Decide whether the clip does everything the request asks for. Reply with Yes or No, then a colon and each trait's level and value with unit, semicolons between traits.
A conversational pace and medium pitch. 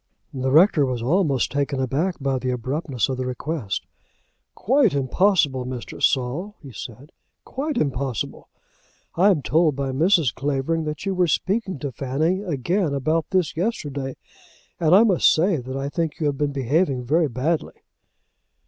Yes: average, 155 wpm; medium, 145 Hz